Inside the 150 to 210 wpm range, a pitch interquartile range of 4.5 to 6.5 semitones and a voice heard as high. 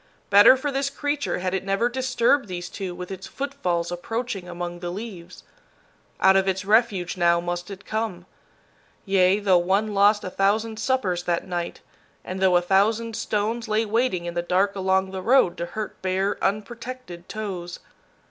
No: average, 170 wpm; average, 3.9 semitones; high, 195 Hz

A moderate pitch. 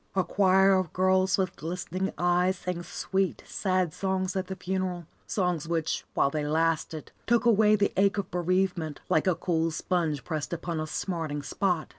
Yes: medium, 180 Hz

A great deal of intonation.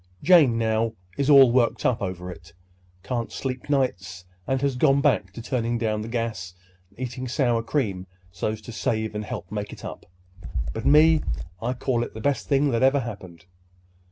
No: average, 3.8 semitones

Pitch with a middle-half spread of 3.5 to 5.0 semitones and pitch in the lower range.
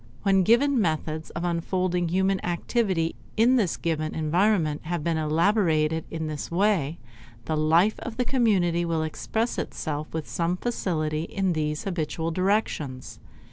No: average, 4.0 semitones; medium, 170 Hz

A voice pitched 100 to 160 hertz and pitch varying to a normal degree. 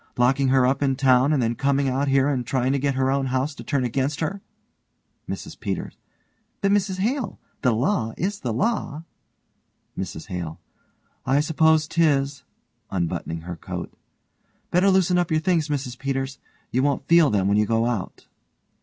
Yes: low, 135 Hz; average, 4.1 semitones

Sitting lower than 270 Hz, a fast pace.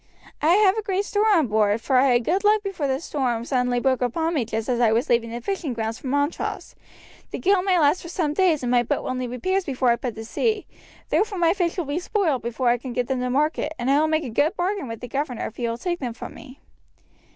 No: very high, 275 Hz; fast, 265 wpm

